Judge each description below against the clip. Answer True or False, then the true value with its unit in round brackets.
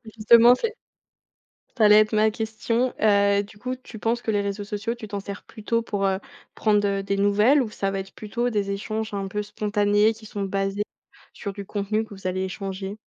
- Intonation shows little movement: True (1.8 semitones)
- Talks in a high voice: True (210 Hz)